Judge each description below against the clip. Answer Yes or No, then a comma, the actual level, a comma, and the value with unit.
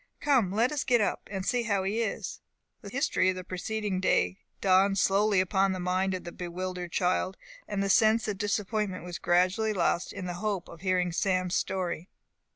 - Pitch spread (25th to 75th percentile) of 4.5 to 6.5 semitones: No, narrow, 2.4 semitones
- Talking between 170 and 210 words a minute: Yes, average, 190 wpm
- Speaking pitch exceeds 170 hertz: Yes, high, 190 Hz